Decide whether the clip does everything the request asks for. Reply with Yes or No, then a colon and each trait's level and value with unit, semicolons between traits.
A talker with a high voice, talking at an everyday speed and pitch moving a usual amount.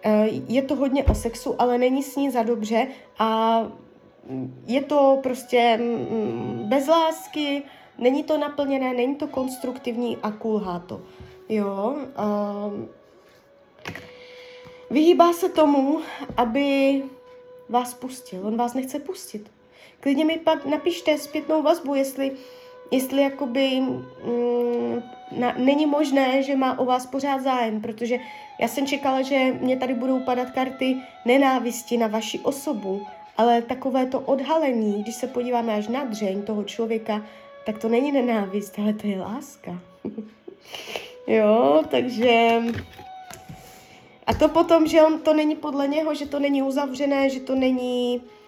Yes: very high, 260 Hz; average, 135 wpm; average, 3.7 semitones